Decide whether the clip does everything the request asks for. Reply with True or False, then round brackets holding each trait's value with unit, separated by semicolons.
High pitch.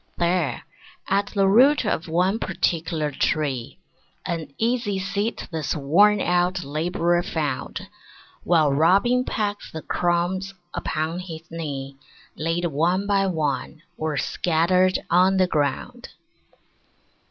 False (175 Hz)